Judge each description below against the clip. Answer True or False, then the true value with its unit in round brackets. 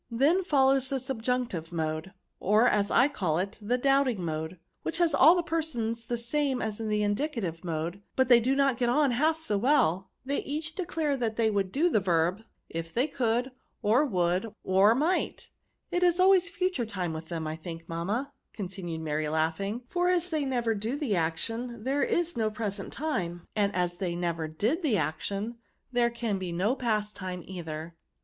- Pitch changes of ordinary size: False (7.2 semitones)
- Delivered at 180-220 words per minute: True (195 wpm)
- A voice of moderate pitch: False (225 Hz)